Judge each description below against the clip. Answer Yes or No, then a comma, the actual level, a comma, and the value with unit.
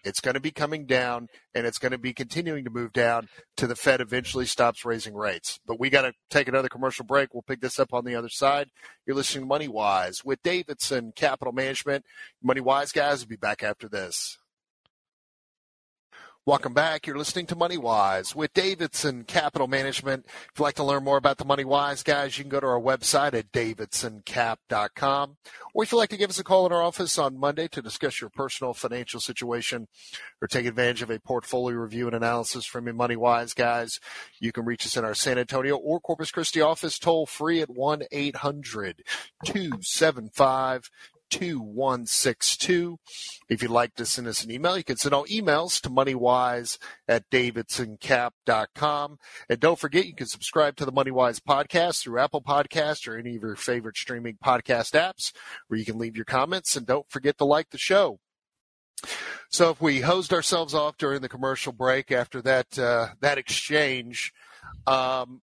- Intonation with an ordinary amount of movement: Yes, average, 3.5 semitones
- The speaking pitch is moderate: No, low, 130 Hz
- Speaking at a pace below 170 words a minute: No, average, 185 wpm